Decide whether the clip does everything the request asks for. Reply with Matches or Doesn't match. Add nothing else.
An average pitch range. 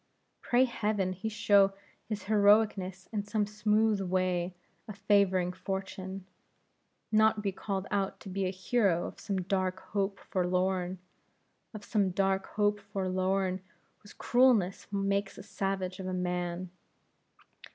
Doesn't match